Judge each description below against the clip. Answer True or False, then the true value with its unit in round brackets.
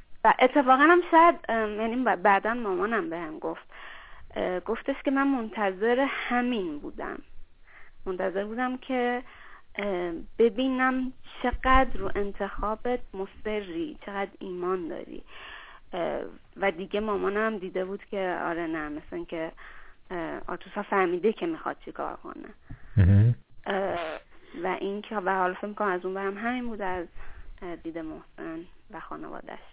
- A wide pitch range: False (4.9 semitones)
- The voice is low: False (205 Hz)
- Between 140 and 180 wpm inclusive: False (120 wpm)